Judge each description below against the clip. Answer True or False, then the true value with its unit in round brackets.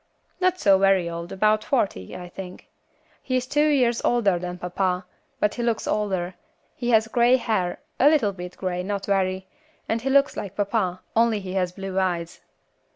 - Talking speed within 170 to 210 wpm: True (180 wpm)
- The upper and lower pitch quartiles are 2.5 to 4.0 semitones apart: False (4.4 semitones)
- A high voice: True (195 Hz)